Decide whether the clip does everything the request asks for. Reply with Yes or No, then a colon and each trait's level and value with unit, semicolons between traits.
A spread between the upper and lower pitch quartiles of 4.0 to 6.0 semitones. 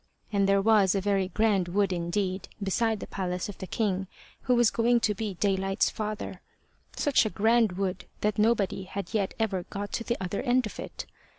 No: narrow, 2.5 semitones